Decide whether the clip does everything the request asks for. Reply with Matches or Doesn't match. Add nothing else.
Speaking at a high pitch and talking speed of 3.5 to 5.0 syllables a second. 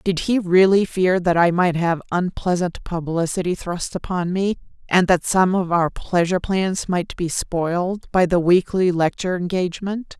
Doesn't match